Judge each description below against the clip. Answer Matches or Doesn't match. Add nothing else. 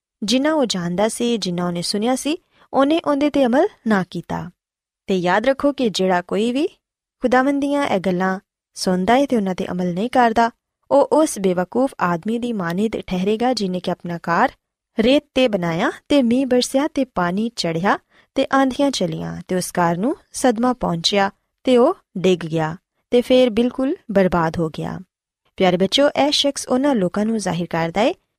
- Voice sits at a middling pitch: Doesn't match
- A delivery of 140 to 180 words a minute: Matches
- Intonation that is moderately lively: Doesn't match